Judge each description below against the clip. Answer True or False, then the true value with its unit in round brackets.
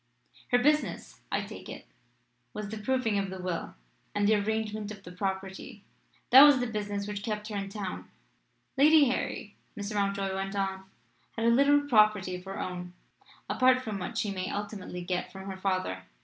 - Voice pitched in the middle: False (205 Hz)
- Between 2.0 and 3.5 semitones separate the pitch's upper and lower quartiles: True (2.5 semitones)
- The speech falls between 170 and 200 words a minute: True (180 wpm)